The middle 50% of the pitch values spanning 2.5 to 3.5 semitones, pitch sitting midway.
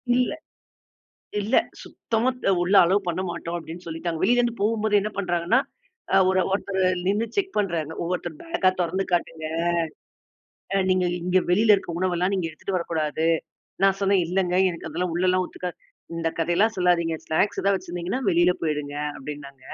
Yes: average, 3.0 semitones; medium, 180 Hz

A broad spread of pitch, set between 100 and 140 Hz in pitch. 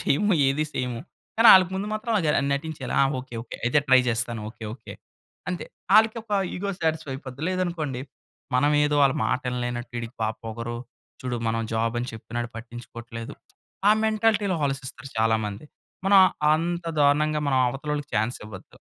Yes: wide, 5.7 semitones; low, 135 Hz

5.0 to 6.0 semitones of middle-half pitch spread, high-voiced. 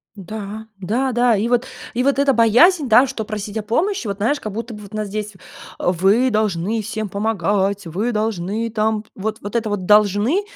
No: narrow, 2.5 semitones; high, 215 Hz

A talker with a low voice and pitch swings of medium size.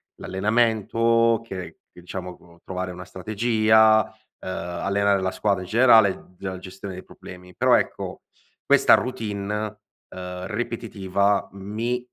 Yes: low, 100 Hz; average, 3.1 semitones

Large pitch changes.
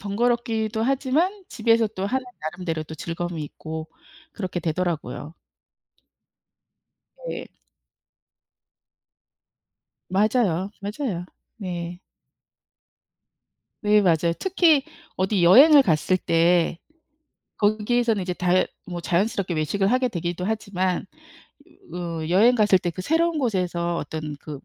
No: average, 5.0 semitones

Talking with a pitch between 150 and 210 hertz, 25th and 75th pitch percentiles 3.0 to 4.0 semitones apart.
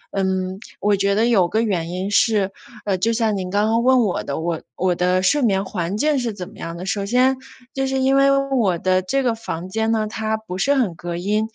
Yes: high, 205 Hz; average, 3.7 semitones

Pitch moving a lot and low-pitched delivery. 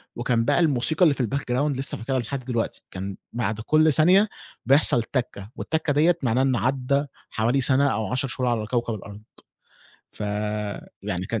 No: average, 4.2 semitones; low, 125 Hz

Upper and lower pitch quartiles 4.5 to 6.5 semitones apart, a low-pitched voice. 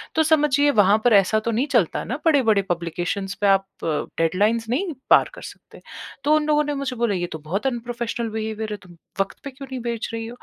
No: average, 5.2 semitones; high, 225 Hz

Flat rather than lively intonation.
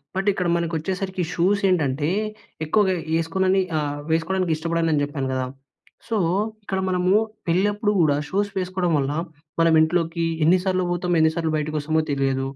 No: average, 3.2 semitones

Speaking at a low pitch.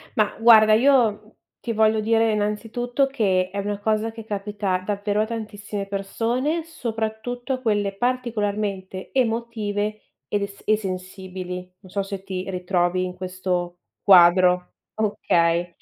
No: high, 205 Hz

